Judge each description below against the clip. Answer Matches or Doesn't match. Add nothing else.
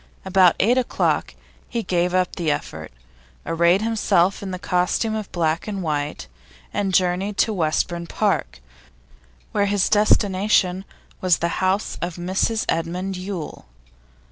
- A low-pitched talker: Doesn't match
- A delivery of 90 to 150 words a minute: Matches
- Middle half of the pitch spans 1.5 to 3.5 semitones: Matches